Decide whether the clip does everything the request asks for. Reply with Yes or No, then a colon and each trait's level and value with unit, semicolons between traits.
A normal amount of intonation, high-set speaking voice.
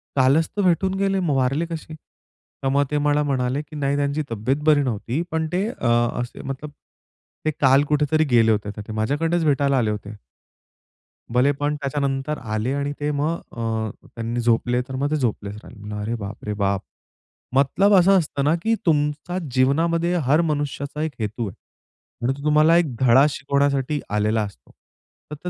No: average, 4.2 semitones; medium, 140 Hz